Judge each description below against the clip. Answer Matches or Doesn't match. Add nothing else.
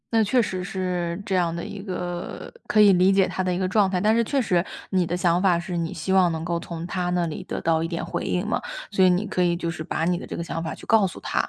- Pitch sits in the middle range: Matches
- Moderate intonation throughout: Doesn't match